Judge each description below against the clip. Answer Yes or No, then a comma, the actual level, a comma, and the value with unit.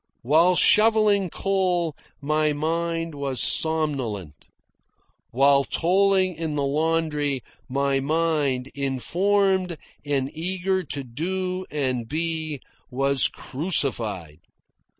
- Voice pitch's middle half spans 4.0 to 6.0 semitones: Yes, average, 4.5 semitones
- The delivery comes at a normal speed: No, slow, 90 wpm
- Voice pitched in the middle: Yes, medium, 155 Hz